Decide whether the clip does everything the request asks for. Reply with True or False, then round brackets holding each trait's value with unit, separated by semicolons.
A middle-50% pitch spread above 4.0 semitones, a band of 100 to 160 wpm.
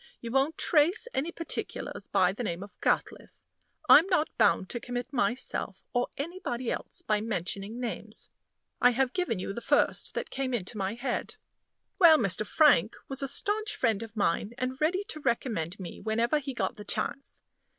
False (5.5 semitones; 175 wpm)